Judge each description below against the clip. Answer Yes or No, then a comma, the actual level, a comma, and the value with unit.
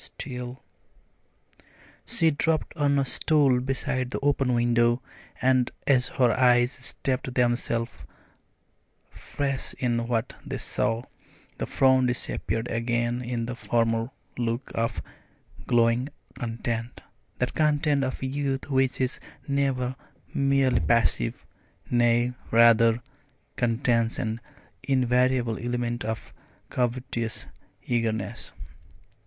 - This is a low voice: Yes, low, 125 Hz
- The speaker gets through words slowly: Yes, slow, 105 wpm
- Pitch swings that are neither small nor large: No, narrow, 2.0 semitones